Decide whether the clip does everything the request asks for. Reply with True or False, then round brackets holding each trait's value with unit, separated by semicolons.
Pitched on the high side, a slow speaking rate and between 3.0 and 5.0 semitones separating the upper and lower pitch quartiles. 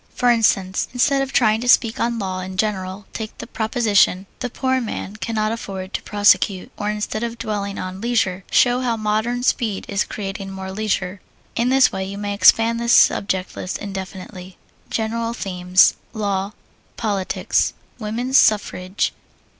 False (210 Hz; 155 wpm; 3.3 semitones)